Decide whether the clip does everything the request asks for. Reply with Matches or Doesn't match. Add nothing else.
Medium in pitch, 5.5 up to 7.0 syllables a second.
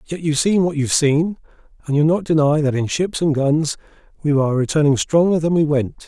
Matches